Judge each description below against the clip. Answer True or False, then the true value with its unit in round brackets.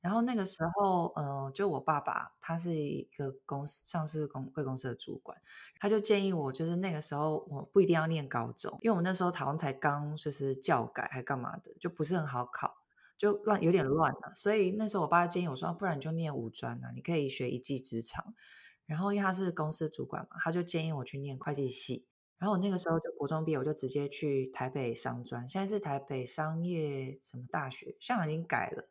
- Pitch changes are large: False (4.7 semitones)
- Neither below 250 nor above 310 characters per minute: False (340 characters per minute)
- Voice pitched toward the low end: False (155 Hz)